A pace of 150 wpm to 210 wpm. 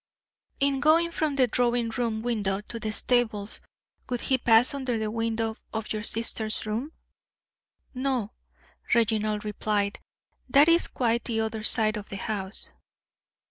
No: average, 140 wpm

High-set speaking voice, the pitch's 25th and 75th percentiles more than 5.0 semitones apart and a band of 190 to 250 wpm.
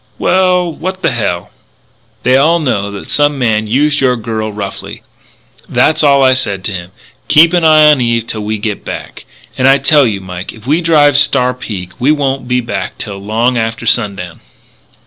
No: low, 125 Hz; wide, 5.5 semitones; average, 195 wpm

